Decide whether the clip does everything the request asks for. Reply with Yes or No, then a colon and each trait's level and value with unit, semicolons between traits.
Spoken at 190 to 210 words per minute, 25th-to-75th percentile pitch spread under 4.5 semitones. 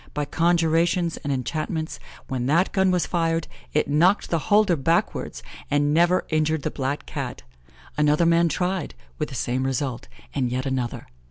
No: average, 160 wpm; average, 3.6 semitones